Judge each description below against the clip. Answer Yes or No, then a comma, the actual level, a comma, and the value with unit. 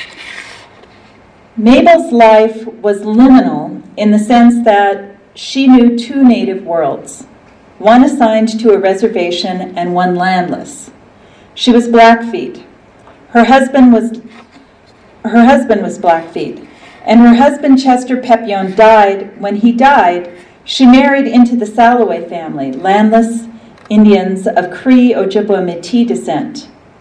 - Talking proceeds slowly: Yes, slow, 120 wpm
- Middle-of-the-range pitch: No, high, 225 Hz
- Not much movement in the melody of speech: No, average, 3.5 semitones